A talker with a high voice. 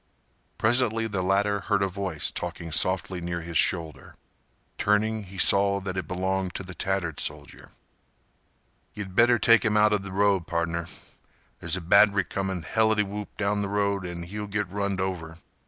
No: very low, 95 Hz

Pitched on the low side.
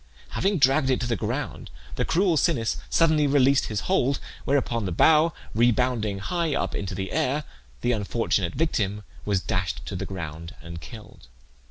Yes: low, 120 Hz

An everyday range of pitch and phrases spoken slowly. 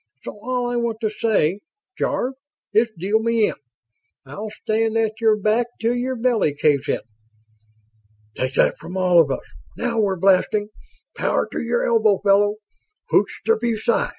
No: average, 3.0 semitones; average, 160 wpm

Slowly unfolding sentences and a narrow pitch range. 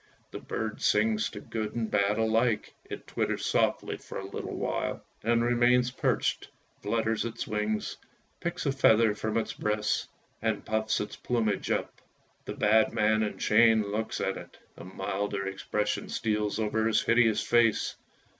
No: average, 155 wpm; narrow, 1.5 semitones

